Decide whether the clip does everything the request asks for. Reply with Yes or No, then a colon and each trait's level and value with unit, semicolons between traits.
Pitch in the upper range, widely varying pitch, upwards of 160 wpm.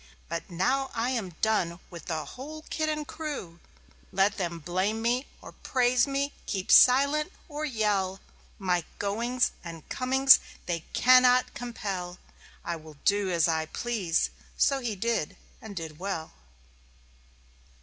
No: high, 210 Hz; wide, 6.4 semitones; slow, 135 wpm